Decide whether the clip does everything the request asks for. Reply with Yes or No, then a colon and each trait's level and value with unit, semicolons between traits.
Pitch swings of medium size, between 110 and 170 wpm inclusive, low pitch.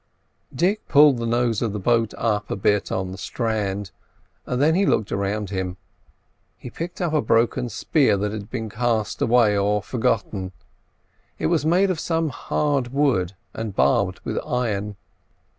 Yes: average, 4.5 semitones; average, 160 wpm; low, 115 Hz